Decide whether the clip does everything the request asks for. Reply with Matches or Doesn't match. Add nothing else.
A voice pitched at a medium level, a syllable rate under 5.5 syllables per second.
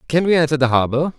Doesn't match